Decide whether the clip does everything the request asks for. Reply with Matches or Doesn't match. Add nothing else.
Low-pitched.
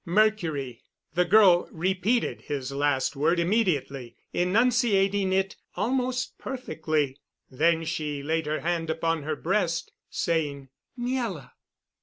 Doesn't match